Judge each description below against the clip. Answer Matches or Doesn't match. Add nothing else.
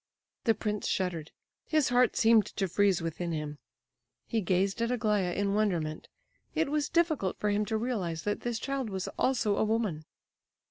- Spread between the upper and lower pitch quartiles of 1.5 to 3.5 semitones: Doesn't match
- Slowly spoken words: Doesn't match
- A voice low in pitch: Doesn't match